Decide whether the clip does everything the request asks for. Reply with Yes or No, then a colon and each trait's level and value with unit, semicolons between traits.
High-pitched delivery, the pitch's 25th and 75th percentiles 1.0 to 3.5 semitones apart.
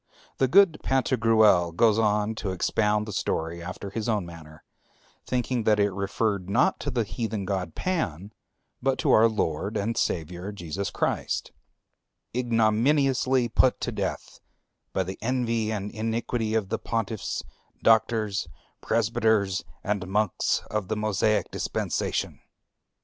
No: low, 110 Hz; average, 2.8 semitones